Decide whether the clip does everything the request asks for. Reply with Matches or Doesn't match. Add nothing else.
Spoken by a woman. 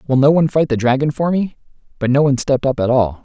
Doesn't match